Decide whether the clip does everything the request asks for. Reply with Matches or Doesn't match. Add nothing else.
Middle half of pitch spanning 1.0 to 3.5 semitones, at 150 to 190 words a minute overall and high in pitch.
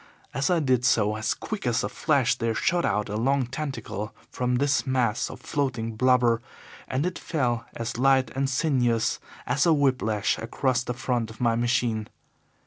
Doesn't match